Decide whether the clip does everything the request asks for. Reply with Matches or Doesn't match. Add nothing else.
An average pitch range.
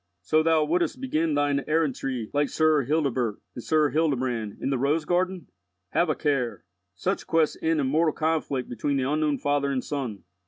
Matches